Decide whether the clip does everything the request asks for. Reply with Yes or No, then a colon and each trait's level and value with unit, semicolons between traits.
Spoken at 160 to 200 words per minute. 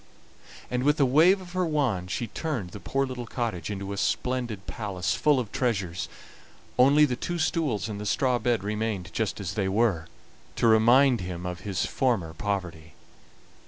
Yes: average, 175 wpm